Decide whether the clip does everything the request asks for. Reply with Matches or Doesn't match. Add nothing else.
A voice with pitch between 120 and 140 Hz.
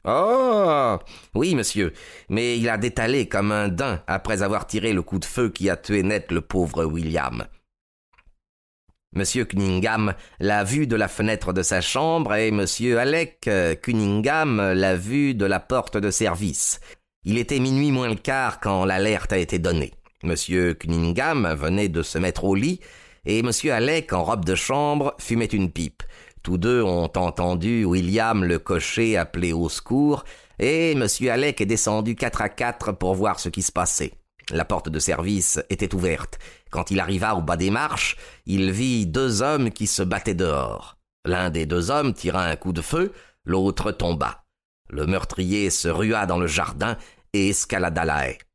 Doesn't match